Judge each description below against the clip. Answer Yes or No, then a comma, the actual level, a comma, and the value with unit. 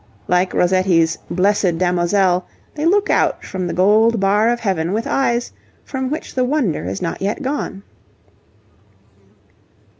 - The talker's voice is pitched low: No, high, 195 Hz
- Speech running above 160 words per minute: No, average, 140 wpm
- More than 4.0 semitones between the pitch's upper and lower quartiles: Yes, average, 5.0 semitones